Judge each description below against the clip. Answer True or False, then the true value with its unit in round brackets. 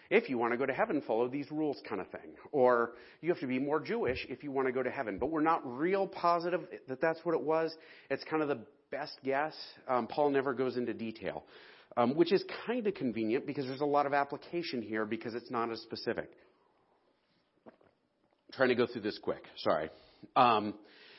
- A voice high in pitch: False (140 Hz)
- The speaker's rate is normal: False (215 wpm)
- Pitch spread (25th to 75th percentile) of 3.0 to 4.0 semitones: False (4.6 semitones)